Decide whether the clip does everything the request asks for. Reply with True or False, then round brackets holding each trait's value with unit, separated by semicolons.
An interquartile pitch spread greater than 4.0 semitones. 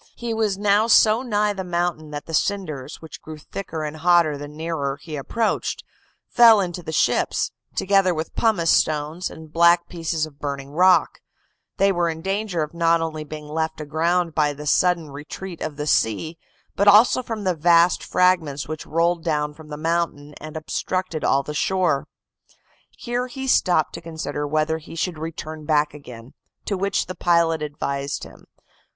False (3.3 semitones)